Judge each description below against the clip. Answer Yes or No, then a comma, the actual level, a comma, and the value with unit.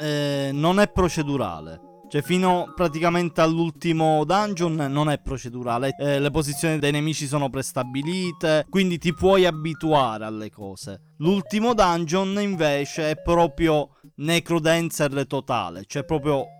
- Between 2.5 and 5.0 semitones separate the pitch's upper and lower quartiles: Yes, average, 3.4 semitones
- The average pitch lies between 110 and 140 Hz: No, medium, 155 Hz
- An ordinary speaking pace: Yes, average, 125 wpm